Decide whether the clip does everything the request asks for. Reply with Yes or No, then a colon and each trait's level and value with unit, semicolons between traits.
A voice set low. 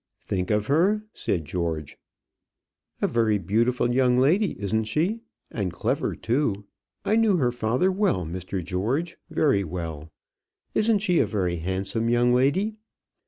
Yes: low, 115 Hz